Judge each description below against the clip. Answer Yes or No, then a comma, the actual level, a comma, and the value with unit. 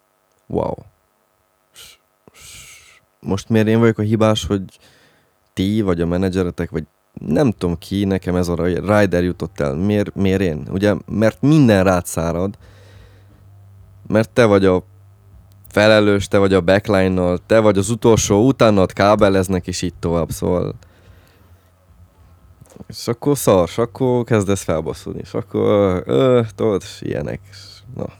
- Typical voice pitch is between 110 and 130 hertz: No, low, 100 Hz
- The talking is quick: No, average, 140 wpm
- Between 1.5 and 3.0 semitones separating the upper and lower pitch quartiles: Yes, average, 2.7 semitones